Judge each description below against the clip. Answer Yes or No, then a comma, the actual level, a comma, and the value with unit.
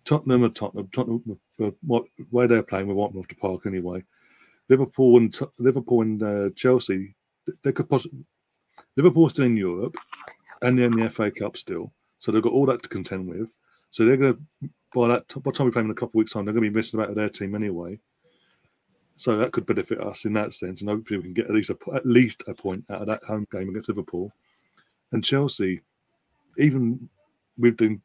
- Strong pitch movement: No, average, 3.4 semitones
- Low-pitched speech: Yes, low, 110 Hz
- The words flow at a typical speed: No, fast, 220 wpm